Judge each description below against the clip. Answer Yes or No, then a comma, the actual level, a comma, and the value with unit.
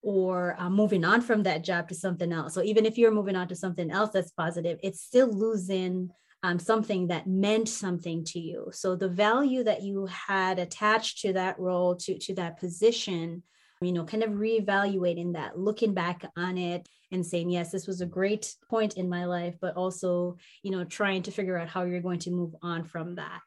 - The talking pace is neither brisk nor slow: No, fast, 210 wpm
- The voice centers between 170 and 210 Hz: Yes, medium, 185 Hz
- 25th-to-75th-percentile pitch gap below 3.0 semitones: Yes, narrow, 2.6 semitones